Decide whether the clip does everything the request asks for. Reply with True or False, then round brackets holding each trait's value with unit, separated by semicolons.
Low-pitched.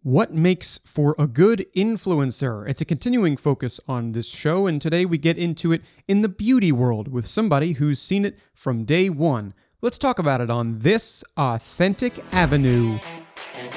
False (160 Hz)